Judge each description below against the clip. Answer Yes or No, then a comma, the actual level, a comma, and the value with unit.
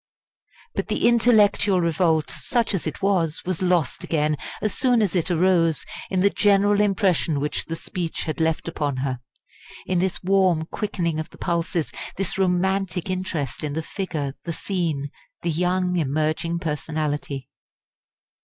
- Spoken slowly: No, average, 150 wpm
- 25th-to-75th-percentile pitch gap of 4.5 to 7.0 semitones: No, average, 3.4 semitones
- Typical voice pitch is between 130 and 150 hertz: No, medium, 175 Hz